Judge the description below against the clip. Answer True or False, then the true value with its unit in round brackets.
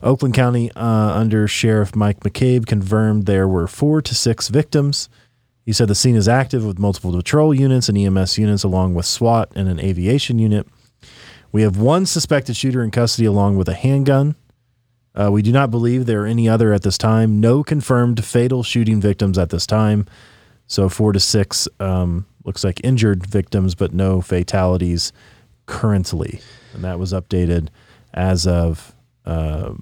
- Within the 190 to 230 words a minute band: False (170 wpm)